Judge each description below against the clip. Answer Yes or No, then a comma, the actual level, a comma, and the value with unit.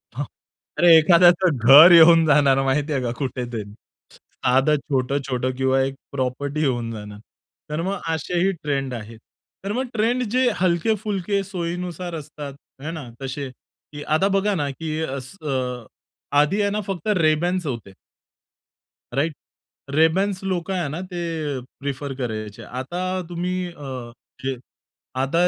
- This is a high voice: No, medium, 150 Hz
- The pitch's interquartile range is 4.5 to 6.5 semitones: Yes, average, 5.0 semitones